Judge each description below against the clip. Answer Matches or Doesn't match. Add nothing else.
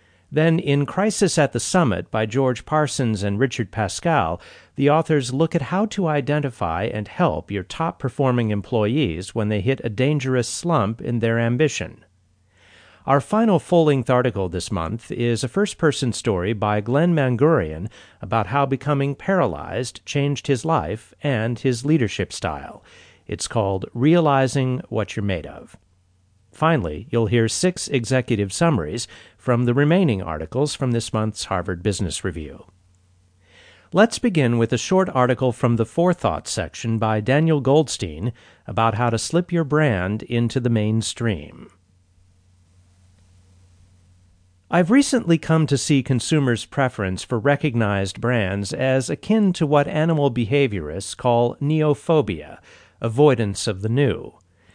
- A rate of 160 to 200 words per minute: Doesn't match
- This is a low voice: Matches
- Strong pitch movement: Matches